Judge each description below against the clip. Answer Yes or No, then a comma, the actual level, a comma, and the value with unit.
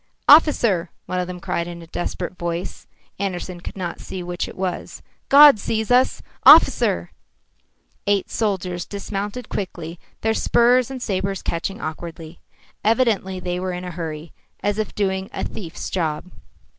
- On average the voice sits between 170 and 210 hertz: Yes, medium, 185 Hz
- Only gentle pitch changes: No, average, 3.2 semitones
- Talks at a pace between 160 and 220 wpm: No, average, 150 wpm